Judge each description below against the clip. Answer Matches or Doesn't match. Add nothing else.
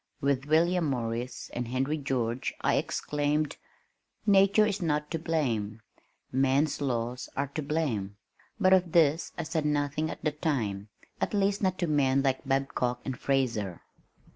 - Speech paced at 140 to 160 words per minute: Matches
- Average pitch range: Matches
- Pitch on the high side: Doesn't match